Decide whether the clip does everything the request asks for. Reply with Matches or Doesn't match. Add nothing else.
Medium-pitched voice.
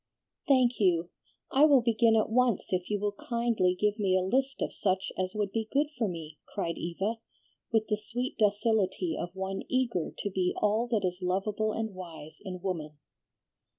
Doesn't match